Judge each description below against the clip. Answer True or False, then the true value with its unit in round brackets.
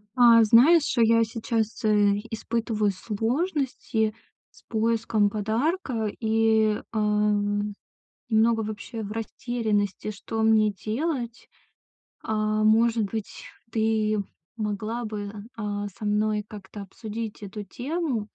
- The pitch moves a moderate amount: False (1.5 semitones)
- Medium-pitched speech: False (220 Hz)